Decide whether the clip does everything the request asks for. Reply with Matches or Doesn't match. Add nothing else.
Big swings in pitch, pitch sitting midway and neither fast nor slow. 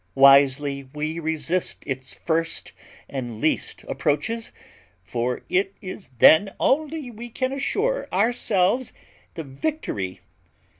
Doesn't match